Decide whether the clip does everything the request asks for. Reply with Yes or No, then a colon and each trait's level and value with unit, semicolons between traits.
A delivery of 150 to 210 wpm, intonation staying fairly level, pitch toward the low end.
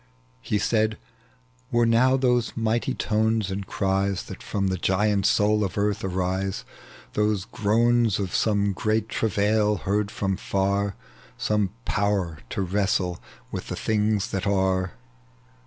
No: slow, 135 wpm; narrow, 2.1 semitones; low, 100 Hz